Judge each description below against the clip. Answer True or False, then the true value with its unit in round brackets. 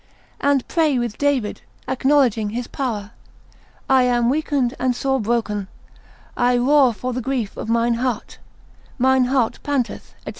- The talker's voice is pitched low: False (250 Hz)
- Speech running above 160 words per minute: False (145 wpm)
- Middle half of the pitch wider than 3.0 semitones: False (2.4 semitones)